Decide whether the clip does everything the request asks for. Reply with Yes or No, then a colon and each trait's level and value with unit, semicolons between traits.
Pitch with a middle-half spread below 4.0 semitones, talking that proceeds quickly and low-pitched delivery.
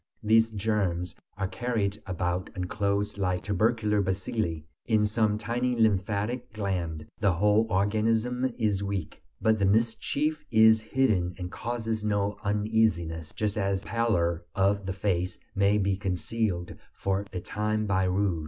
No: average, 2.7 semitones; average, 140 wpm; low, 105 Hz